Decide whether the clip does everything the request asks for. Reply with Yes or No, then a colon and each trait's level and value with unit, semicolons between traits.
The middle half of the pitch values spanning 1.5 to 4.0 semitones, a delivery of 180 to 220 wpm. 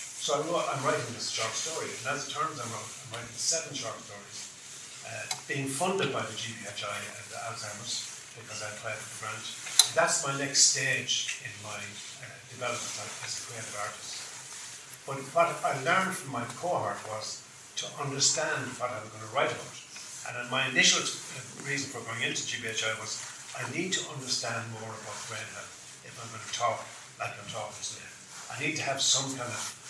No: average, 4.4 semitones; average, 190 wpm